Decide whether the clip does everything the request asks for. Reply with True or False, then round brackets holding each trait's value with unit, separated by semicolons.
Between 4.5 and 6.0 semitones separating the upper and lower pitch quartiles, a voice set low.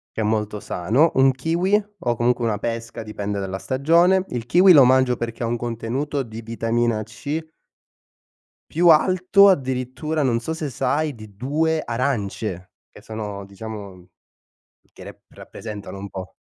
True (5.5 semitones; 120 Hz)